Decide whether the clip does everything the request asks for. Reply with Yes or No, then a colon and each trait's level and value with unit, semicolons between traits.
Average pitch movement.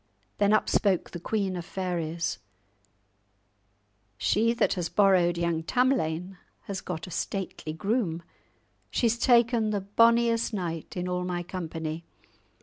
Yes: average, 4.1 semitones